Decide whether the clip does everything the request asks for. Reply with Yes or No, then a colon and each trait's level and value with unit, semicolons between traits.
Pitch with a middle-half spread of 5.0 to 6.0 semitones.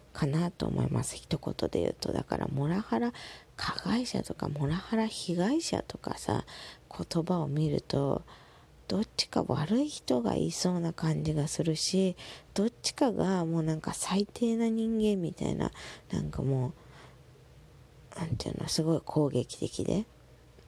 Yes: wide, 5.4 semitones